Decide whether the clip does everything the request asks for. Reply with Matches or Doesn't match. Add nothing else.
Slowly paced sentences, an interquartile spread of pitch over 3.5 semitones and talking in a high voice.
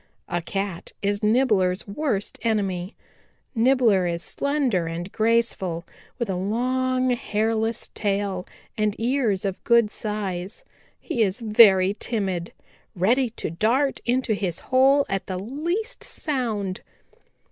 Matches